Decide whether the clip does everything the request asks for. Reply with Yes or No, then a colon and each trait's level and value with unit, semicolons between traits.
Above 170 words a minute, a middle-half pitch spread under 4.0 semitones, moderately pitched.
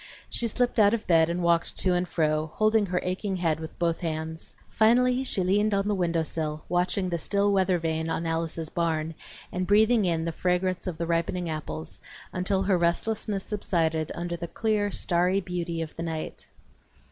Yes: average, 185 wpm; average, 3.4 semitones; medium, 175 Hz